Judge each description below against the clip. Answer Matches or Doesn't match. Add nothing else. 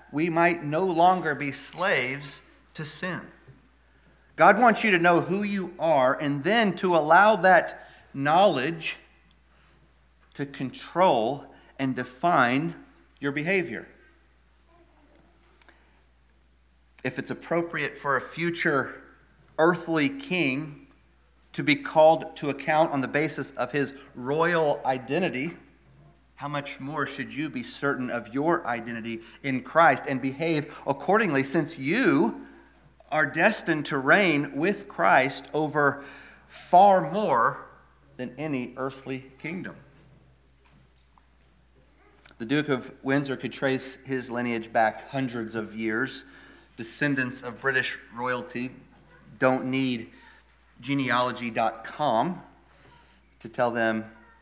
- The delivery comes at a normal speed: Doesn't match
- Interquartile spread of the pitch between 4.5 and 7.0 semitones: Matches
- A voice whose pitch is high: Doesn't match